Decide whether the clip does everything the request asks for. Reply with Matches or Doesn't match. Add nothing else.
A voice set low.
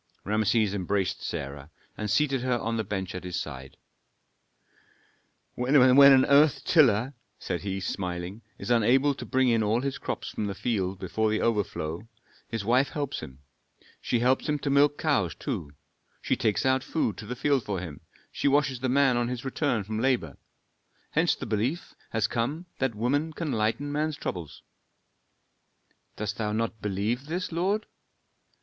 Matches